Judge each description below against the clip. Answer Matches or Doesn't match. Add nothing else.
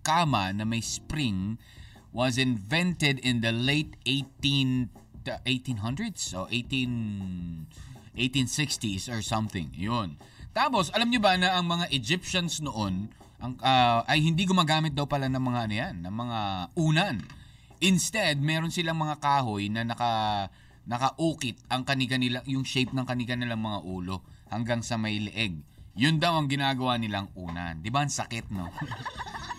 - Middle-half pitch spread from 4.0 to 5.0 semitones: Matches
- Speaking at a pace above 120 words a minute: Matches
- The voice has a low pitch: Matches